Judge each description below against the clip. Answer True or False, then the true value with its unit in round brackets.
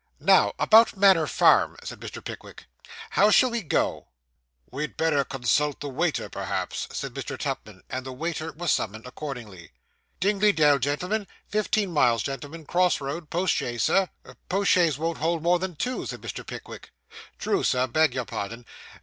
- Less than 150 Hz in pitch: False (155 Hz)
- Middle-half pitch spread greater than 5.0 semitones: True (5.5 semitones)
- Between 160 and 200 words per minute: True (170 wpm)